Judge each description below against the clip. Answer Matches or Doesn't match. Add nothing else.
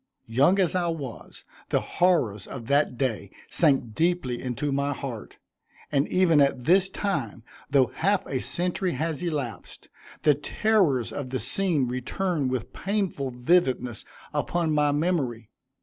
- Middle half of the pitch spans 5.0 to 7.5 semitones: Matches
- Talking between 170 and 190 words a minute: Doesn't match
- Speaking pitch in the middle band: Matches